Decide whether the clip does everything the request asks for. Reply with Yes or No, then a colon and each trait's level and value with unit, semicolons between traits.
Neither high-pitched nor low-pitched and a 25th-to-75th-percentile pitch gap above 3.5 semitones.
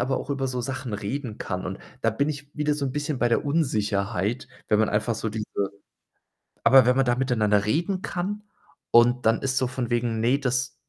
No: low, 125 Hz; average, 3.9 semitones